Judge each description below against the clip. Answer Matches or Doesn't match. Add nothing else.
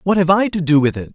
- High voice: Doesn't match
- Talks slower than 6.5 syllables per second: Doesn't match